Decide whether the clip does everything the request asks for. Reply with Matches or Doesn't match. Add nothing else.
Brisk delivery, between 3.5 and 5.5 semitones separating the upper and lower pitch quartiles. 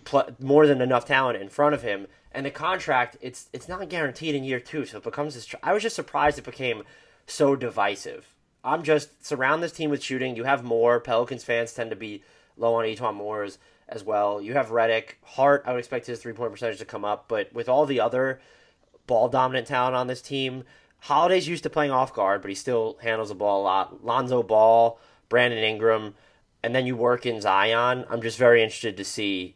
Matches